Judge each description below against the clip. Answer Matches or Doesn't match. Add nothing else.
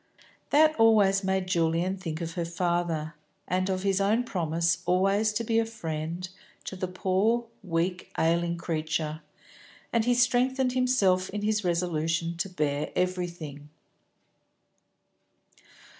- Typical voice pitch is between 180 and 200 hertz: Matches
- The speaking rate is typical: Doesn't match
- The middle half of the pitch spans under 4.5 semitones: Matches